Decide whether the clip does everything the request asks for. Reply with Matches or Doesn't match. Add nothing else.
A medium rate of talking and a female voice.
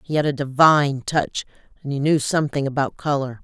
Matches